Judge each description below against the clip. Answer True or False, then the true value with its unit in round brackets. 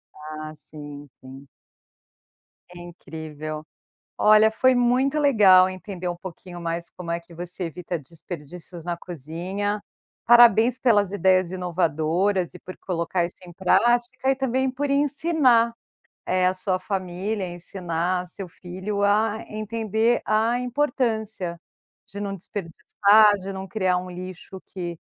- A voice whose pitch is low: False (185 Hz)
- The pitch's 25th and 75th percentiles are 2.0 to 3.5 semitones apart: False (4.1 semitones)